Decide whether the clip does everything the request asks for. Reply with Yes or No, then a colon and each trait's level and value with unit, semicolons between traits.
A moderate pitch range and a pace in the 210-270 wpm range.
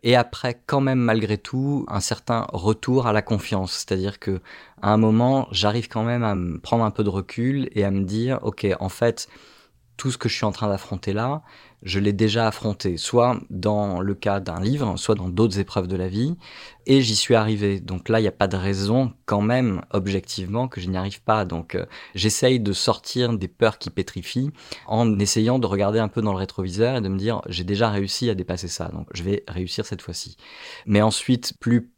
Yes: average, 3.6 semitones; fast, 220 wpm